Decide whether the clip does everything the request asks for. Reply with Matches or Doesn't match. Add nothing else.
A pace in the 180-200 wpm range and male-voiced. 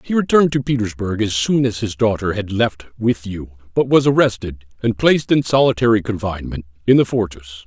Matches